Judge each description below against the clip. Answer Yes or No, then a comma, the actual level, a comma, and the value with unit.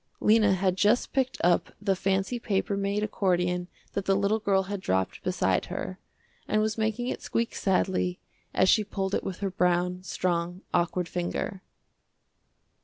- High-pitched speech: Yes, high, 195 Hz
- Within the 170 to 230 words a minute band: No, average, 160 wpm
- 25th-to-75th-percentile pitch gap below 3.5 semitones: Yes, narrow, 2.5 semitones